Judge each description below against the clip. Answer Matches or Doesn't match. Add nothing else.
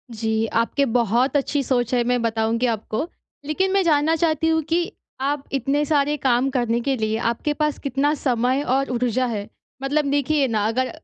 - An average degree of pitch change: Matches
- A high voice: Matches